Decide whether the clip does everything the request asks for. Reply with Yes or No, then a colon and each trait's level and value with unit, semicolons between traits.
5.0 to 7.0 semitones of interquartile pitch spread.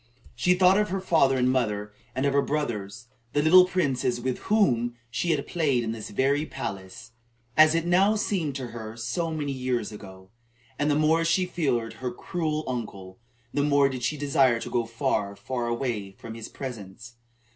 Yes: average, 5.3 semitones